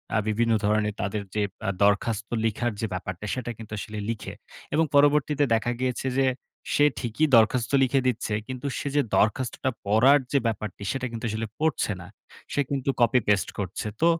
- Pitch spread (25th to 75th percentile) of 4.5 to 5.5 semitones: No, average, 3.8 semitones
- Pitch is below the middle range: Yes, low, 115 Hz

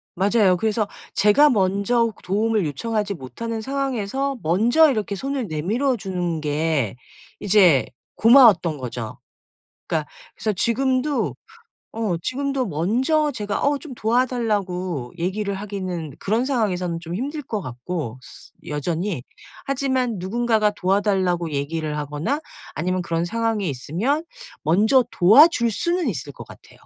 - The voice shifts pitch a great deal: Yes, wide, 6.1 semitones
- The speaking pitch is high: Yes, high, 205 Hz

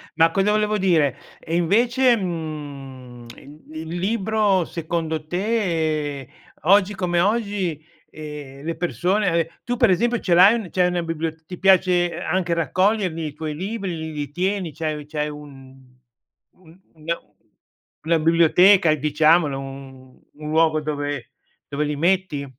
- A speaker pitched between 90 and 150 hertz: No, medium, 165 Hz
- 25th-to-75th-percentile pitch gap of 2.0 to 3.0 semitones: No, average, 3.9 semitones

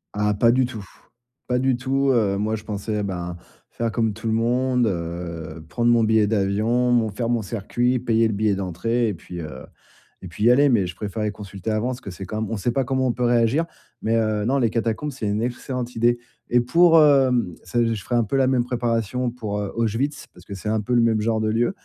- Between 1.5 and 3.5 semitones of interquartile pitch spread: Yes, average, 2.9 semitones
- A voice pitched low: Yes, low, 115 Hz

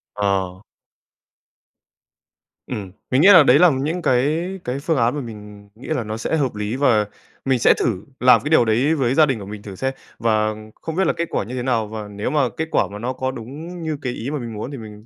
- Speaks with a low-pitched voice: Yes, low, 125 Hz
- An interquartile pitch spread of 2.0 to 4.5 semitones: No, average, 4.9 semitones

